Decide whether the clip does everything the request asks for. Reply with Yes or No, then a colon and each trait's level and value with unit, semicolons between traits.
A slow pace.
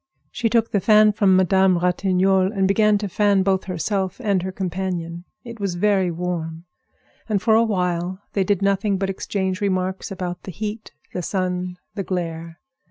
No: average, 170 wpm